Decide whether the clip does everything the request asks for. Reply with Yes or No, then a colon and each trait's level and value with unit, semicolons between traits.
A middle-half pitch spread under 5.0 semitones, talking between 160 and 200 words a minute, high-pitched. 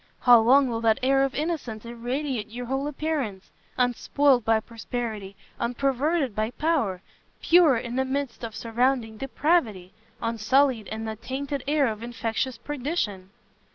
No: average, 3.8 semitones; average, 140 wpm; high, 245 Hz